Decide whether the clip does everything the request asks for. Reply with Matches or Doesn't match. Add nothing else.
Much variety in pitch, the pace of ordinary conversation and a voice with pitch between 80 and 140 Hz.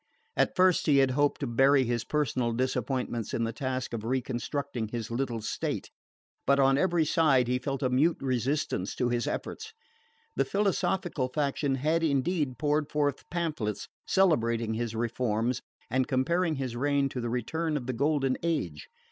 Doesn't match